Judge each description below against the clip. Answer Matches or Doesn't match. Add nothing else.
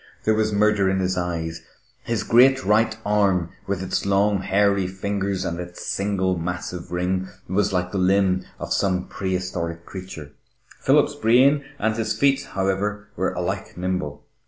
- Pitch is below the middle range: Matches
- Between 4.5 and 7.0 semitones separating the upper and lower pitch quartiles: Doesn't match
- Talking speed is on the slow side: Doesn't match